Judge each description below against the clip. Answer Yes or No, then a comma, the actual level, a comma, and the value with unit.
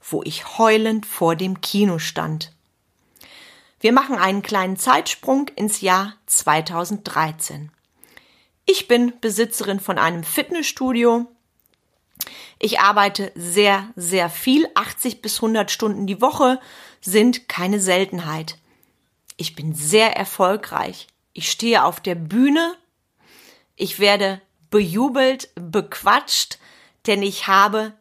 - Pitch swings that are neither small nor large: Yes, average, 4.1 semitones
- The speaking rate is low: Yes, slow, 110 wpm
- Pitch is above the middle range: Yes, high, 205 Hz